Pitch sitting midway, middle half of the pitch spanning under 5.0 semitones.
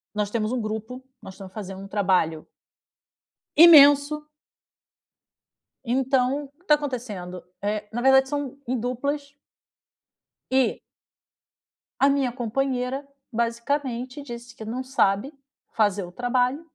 No: very high, 250 Hz; average, 4.4 semitones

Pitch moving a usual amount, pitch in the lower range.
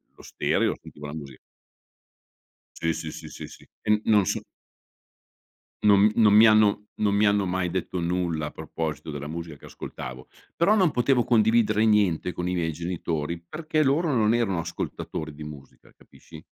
Yes: average, 5.0 semitones; very low, 95 Hz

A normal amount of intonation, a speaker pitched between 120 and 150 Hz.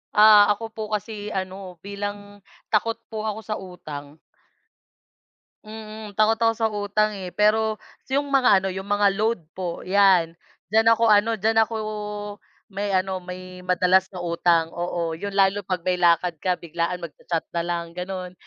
No: average, 3.0 semitones; high, 195 Hz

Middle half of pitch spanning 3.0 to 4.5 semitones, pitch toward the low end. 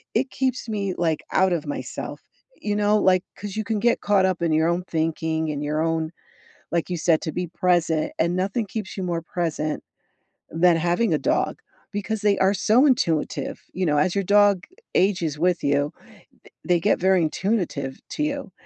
No: average, 4.1 semitones; medium, 180 Hz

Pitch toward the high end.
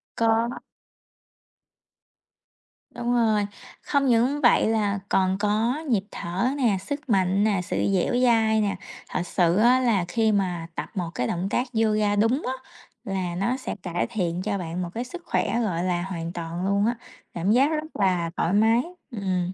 Yes: high, 205 Hz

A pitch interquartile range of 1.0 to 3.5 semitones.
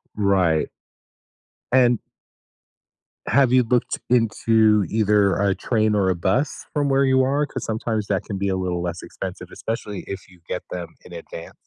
No: average, 4.4 semitones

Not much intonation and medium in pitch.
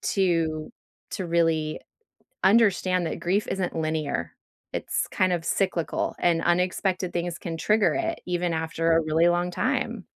Yes: narrow, 2.2 semitones; medium, 175 Hz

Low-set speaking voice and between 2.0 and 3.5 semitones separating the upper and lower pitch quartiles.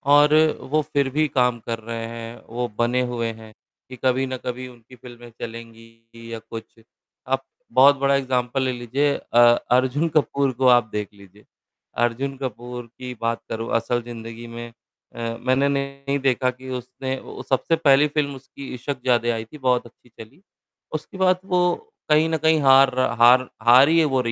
Yes: low, 125 Hz; average, 2.8 semitones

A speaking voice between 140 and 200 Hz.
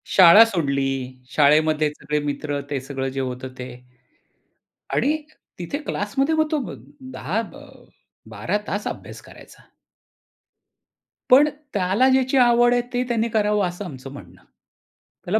Yes: medium, 185 Hz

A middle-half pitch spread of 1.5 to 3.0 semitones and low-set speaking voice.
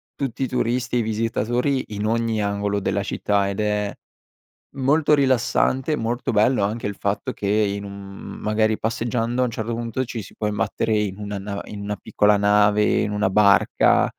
Yes: narrow, 2.6 semitones; low, 105 Hz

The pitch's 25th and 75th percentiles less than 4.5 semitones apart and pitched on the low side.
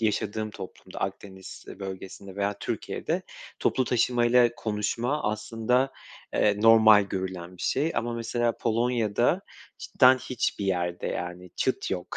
Yes: average, 3.8 semitones; low, 110 Hz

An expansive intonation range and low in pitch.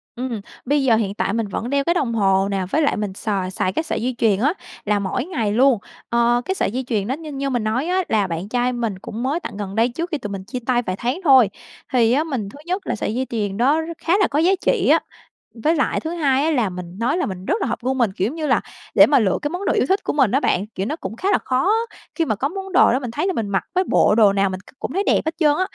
No: wide, 6.5 semitones; high, 245 Hz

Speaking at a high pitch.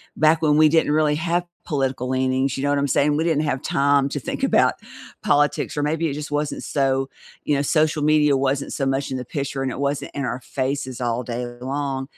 No: medium, 140 Hz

